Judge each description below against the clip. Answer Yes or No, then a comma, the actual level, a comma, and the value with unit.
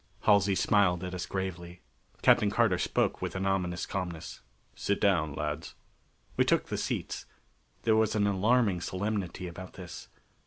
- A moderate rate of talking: Yes, average, 150 wpm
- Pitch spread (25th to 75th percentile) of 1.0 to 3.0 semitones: Yes, narrow, 2.5 semitones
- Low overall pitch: Yes, very low, 95 Hz